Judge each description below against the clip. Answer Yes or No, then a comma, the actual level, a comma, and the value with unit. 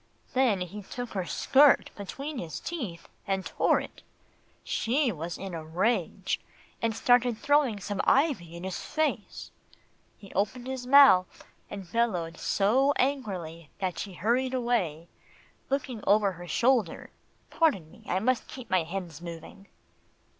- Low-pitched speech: No, high, 205 Hz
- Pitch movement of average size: No, wide, 6.3 semitones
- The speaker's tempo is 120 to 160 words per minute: Yes, average, 140 wpm